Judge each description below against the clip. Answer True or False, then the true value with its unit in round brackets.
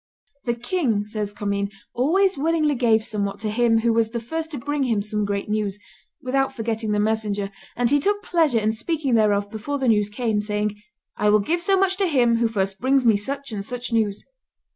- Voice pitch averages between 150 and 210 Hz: False (230 Hz)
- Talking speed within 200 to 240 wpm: True (205 wpm)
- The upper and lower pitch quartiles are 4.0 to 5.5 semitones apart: True (4.7 semitones)